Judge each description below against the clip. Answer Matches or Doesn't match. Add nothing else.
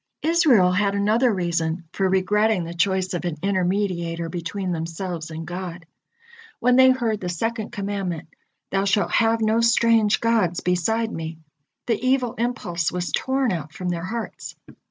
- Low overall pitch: Doesn't match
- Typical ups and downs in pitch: Matches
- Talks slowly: Doesn't match